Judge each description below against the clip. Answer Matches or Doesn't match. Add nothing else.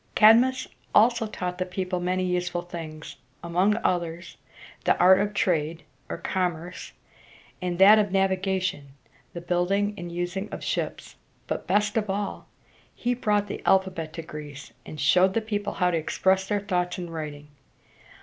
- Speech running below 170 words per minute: Matches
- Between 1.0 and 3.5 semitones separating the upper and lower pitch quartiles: Matches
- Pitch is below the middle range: Doesn't match